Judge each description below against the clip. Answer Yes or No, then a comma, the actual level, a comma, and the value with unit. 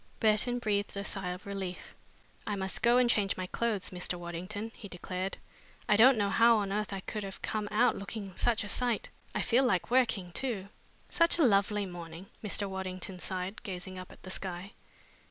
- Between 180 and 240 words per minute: Yes, average, 195 wpm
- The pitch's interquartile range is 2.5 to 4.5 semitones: Yes, average, 3.1 semitones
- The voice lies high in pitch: Yes, high, 200 Hz